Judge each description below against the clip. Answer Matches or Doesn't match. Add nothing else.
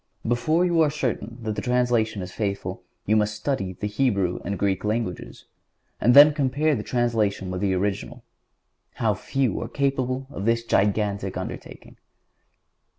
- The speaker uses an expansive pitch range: Doesn't match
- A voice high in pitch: Doesn't match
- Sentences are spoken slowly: Doesn't match